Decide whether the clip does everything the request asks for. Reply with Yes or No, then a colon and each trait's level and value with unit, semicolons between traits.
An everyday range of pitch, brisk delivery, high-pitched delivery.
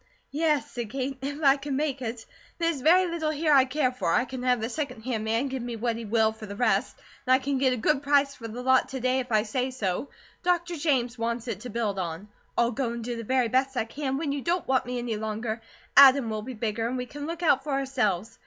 Yes: average, 3.5 semitones; fast, 265 wpm; very high, 255 Hz